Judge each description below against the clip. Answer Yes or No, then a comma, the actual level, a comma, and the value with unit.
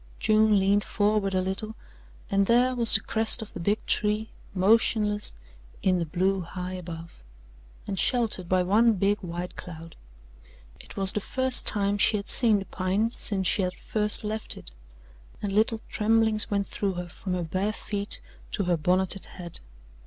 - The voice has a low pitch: No, high, 200 Hz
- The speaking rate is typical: Yes, average, 170 wpm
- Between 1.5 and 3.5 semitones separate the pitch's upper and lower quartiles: Yes, average, 2.7 semitones